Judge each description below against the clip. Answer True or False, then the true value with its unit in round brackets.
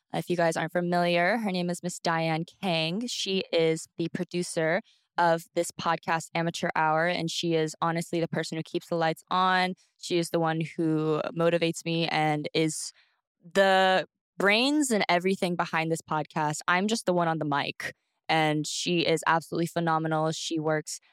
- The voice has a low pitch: False (170 Hz)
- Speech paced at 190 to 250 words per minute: False (175 wpm)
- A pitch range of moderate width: False (1.7 semitones)